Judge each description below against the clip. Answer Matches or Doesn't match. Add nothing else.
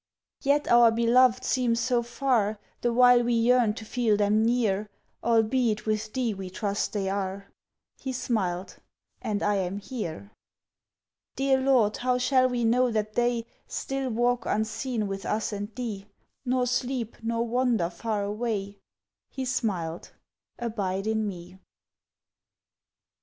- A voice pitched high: Matches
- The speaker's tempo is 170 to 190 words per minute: Doesn't match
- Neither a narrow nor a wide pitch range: Matches